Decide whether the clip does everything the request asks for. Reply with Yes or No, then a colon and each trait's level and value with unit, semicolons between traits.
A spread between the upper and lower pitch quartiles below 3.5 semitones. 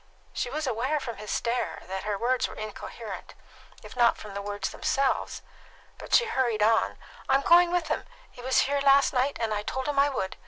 No: average, 4.5 semitones